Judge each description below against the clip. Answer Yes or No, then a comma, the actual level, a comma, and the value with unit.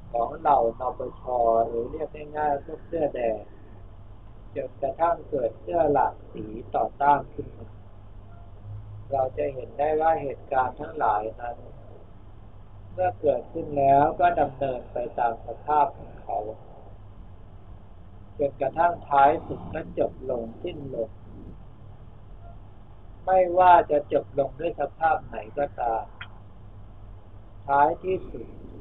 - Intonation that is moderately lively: No, wide, 6.1 semitones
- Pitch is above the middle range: No, low, 115 Hz